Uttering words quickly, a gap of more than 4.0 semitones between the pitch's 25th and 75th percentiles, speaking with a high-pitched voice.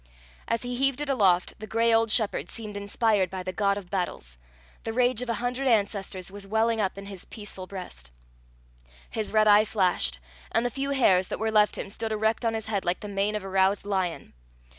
No: fast, 215 wpm; average, 2.8 semitones; high, 210 Hz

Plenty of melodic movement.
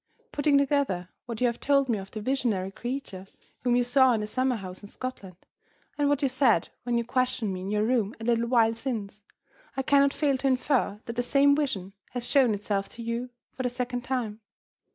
No: average, 3.8 semitones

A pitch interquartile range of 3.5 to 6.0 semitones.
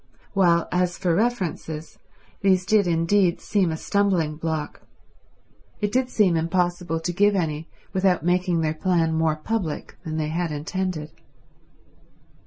No: average, 2.8 semitones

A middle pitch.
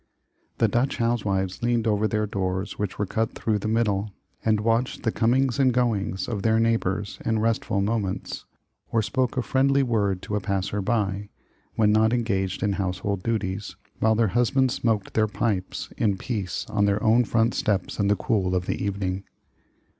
No: low, 105 Hz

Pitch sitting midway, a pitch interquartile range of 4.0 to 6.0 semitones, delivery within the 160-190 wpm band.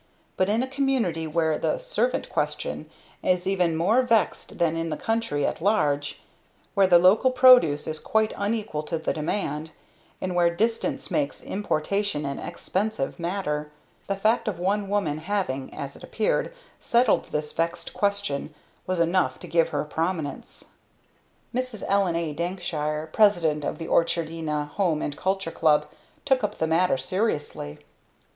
No: medium, 175 Hz; average, 5.0 semitones; average, 150 wpm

